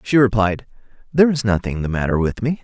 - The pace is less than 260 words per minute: Yes, fast, 205 wpm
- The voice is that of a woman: No, male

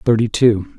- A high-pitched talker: No, low, 110 Hz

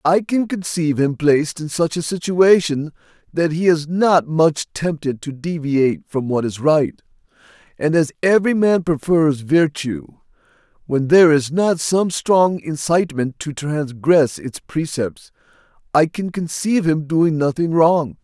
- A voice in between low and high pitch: Yes, medium, 160 Hz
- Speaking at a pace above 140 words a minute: Yes, average, 150 wpm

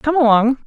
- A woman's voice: Yes, female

